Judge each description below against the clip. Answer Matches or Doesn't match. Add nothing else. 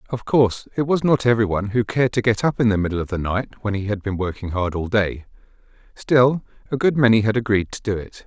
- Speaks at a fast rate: Matches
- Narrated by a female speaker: Doesn't match